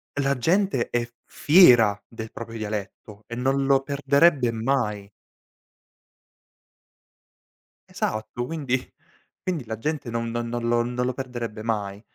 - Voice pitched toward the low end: Yes, low, 120 Hz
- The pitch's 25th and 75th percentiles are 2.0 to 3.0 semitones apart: No, average, 3.5 semitones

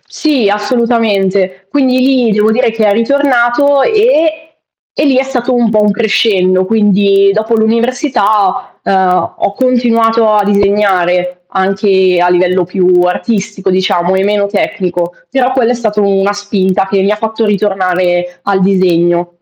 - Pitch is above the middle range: Yes, high, 205 Hz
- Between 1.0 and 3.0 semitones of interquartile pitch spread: No, average, 3.7 semitones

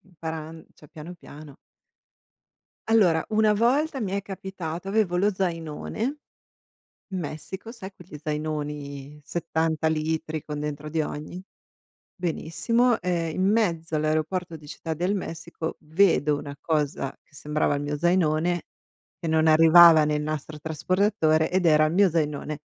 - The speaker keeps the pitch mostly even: No, average, 3.2 semitones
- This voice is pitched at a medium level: Yes, medium, 160 Hz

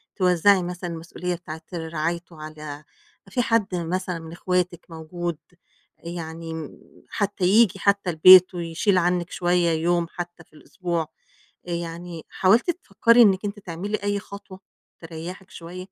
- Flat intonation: Yes, narrow, 2.3 semitones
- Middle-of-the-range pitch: Yes, medium, 175 Hz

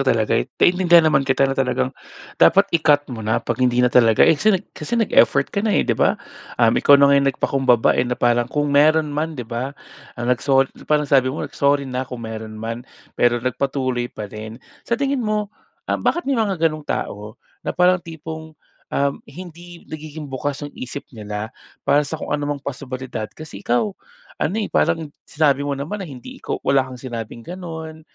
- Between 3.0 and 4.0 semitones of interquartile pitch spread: No, average, 4.4 semitones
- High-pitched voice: No, medium, 140 Hz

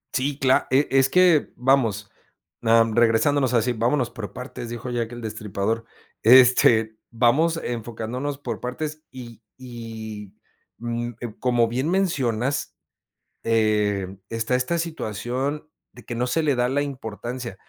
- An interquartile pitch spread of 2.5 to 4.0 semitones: Yes, average, 2.9 semitones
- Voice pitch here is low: Yes, low, 120 Hz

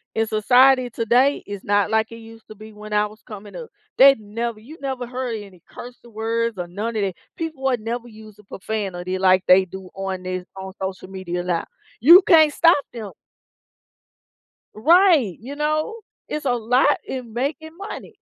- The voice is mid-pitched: No, high, 225 Hz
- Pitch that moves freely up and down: No, average, 4.6 semitones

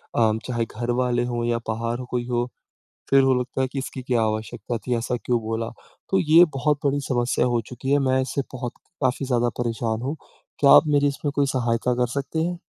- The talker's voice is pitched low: Yes, low, 125 Hz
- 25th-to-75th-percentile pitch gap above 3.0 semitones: No, narrow, 2.5 semitones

